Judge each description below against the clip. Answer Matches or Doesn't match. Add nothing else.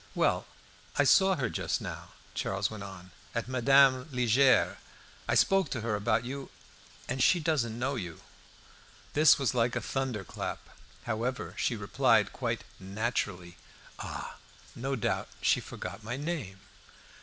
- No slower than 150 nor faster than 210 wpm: Doesn't match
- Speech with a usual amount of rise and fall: Matches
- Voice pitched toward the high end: Doesn't match